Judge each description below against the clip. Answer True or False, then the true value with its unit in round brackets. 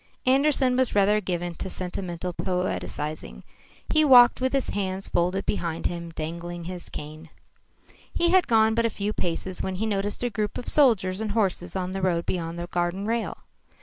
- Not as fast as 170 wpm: False (180 wpm)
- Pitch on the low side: False (190 Hz)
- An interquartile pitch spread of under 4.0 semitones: False (4.3 semitones)